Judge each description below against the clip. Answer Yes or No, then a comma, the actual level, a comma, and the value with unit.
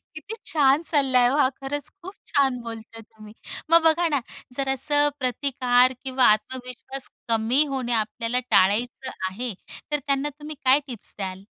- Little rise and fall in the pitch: No, average, 3.4 semitones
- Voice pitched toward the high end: Yes, very high, 260 Hz